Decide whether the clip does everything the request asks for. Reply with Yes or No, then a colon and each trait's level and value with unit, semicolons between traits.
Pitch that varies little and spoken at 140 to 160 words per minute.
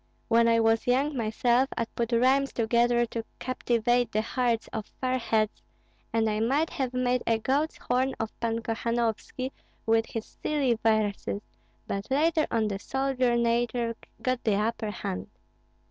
Yes: narrow, 2.2 semitones; average, 155 wpm